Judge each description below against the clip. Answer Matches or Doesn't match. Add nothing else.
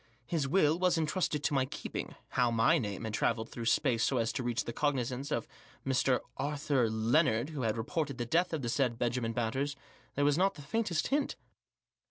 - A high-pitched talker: Doesn't match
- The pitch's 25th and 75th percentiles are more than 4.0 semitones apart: Matches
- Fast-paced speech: Matches